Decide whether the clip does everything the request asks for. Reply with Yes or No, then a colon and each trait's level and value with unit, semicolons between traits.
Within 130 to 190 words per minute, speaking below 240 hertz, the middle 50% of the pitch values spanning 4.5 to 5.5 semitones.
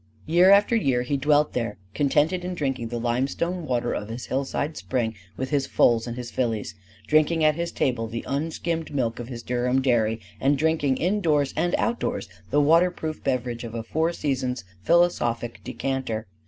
Yes: average, 170 wpm; low, 135 Hz; average, 4.9 semitones